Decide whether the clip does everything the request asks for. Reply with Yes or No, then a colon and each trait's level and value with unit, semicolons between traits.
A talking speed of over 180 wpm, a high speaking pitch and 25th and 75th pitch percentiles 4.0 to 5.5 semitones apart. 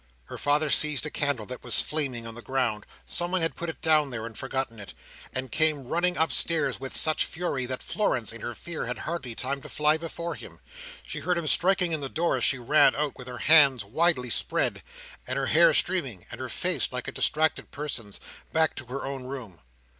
No: fast, 205 wpm; medium, 140 Hz; average, 4.3 semitones